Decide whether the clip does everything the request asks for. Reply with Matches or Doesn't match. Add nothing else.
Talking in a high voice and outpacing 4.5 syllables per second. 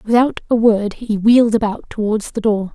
Matches